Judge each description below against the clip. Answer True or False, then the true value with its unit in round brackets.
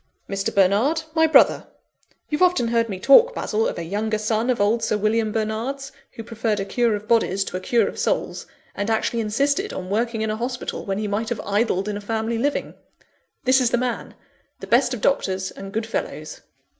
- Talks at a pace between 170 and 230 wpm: True (205 wpm)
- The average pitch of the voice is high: True (225 Hz)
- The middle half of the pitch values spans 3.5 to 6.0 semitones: False (2.8 semitones)